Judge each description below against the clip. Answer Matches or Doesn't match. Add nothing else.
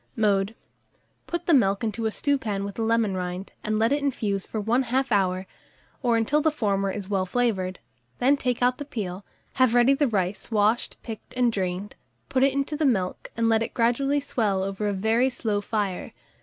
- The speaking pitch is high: Matches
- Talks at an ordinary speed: Matches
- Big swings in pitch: Doesn't match